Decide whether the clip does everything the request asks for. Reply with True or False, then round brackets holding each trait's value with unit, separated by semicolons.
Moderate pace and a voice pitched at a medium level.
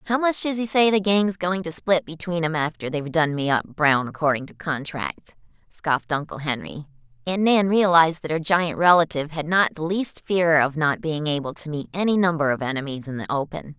False (215 wpm; 165 Hz)